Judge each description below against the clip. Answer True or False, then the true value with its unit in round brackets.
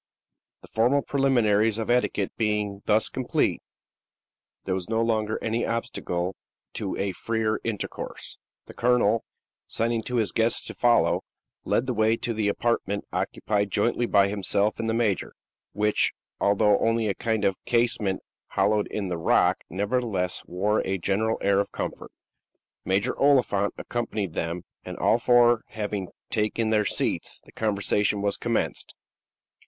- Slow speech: False (145 wpm)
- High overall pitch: False (110 Hz)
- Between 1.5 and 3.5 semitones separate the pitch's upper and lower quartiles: True (2.4 semitones)